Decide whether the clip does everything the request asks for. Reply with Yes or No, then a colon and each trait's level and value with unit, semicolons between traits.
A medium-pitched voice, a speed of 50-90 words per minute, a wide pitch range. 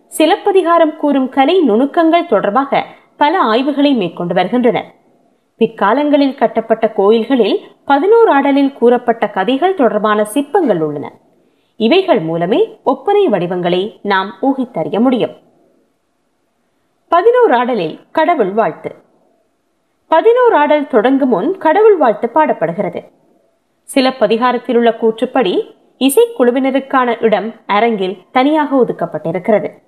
No: very high, 255 Hz; average, 85 wpm; wide, 6.2 semitones